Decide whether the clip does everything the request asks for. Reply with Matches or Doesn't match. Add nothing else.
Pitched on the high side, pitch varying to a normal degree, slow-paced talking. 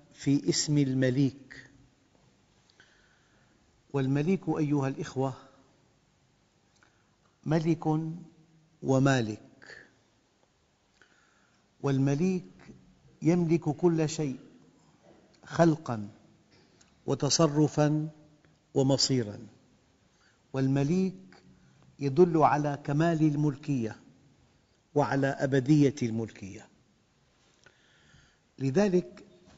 Doesn't match